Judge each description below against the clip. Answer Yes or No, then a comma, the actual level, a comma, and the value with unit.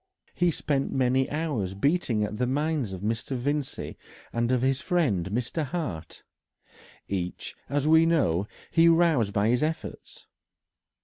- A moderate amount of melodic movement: No, wide, 6.7 semitones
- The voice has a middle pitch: No, low, 130 Hz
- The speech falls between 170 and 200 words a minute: No, average, 140 wpm